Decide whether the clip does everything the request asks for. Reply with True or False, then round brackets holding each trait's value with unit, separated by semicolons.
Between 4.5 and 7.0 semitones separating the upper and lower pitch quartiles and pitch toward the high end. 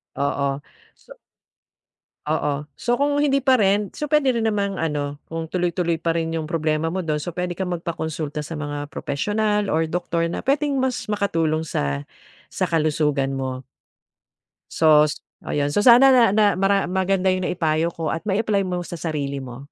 False (4.9 semitones; 165 Hz)